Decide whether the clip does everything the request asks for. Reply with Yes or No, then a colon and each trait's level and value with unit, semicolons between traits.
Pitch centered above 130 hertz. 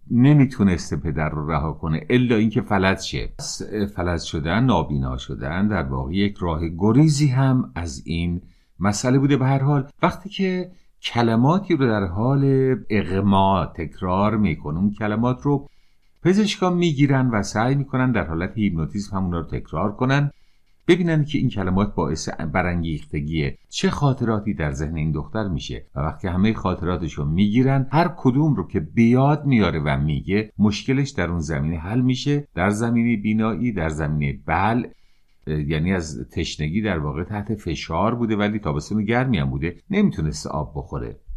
No: low, 105 Hz